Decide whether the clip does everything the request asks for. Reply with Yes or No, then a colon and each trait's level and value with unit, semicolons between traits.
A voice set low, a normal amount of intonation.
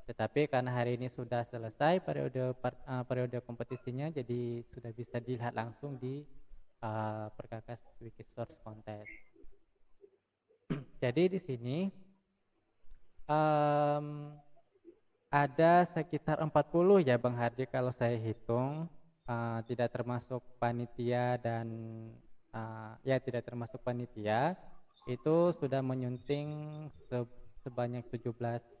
Yes: low, 125 Hz; average, 3.8 semitones